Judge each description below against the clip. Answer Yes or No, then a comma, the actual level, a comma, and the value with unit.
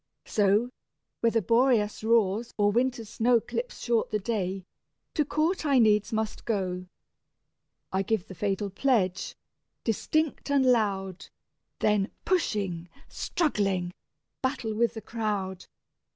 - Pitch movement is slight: No, average, 3.7 semitones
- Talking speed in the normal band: No, slow, 120 wpm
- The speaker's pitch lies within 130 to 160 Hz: No, high, 215 Hz